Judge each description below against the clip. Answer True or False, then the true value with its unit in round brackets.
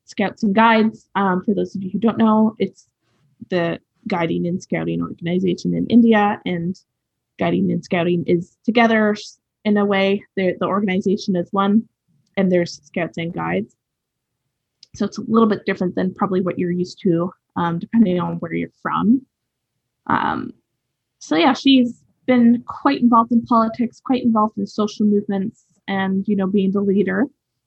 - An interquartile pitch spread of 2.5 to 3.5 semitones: False (3.9 semitones)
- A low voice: False (195 Hz)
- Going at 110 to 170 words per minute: True (165 wpm)